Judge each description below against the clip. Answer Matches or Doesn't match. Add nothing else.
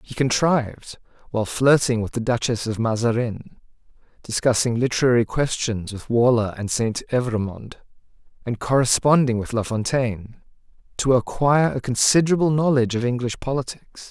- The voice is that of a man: Matches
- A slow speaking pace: Matches